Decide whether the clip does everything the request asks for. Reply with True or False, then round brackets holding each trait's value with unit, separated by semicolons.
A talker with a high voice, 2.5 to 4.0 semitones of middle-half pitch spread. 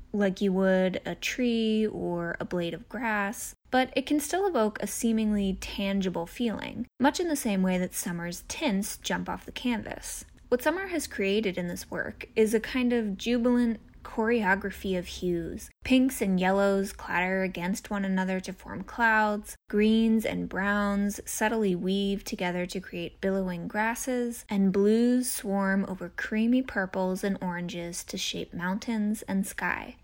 True (205 Hz; 3.5 semitones)